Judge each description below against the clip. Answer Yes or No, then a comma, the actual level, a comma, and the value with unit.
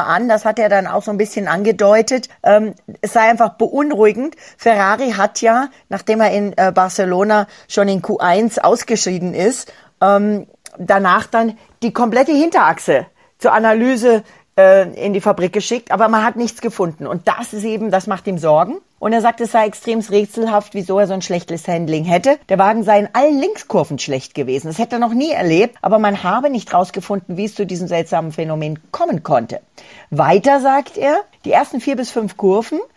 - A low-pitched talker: No, high, 210 Hz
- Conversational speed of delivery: Yes, average, 180 wpm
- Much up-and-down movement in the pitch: No, average, 3.4 semitones